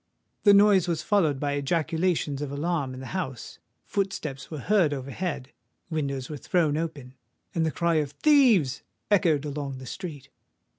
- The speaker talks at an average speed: Yes, average, 150 wpm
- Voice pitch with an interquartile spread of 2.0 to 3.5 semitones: No, average, 4.3 semitones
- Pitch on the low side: No, medium, 150 Hz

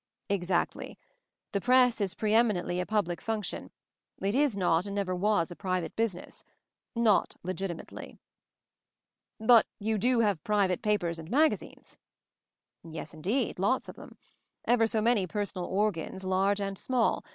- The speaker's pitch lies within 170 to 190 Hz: No, high, 200 Hz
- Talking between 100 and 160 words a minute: Yes, average, 150 wpm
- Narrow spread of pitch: No, average, 3.4 semitones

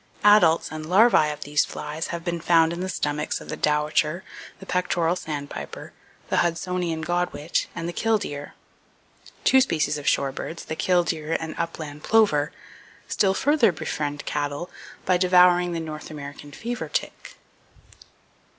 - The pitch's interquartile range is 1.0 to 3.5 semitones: Yes, average, 3.1 semitones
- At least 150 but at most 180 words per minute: No, average, 140 wpm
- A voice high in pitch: No, medium, 165 Hz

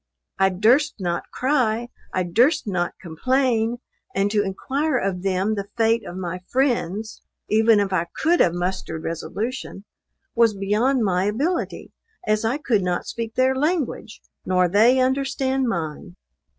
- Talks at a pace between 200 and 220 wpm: No, average, 145 wpm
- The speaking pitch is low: No, high, 220 Hz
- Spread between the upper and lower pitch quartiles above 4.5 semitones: Yes, wide, 5.5 semitones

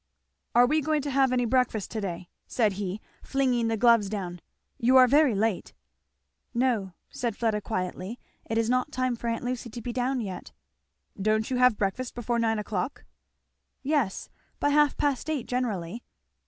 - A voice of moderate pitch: No, high, 235 Hz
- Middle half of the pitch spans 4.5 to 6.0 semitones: No, average, 3.3 semitones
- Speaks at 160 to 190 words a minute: Yes, average, 170 wpm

